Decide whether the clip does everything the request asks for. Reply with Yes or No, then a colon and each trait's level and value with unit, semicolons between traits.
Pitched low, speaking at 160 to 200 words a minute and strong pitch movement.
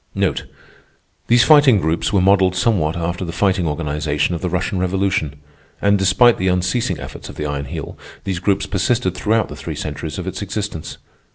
No: very low, 95 Hz; average, 175 wpm; average, 3.6 semitones